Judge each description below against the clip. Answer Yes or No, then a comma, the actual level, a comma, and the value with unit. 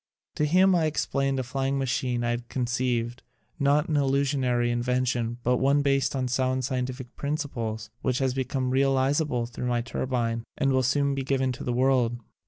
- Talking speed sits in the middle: Yes, average, 185 wpm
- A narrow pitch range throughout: Yes, narrow, 2.1 semitones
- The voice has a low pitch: Yes, low, 130 Hz